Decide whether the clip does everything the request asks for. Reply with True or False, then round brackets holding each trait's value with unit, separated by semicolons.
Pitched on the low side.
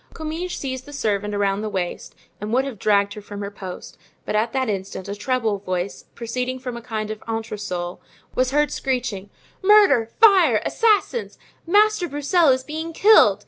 False (235 Hz)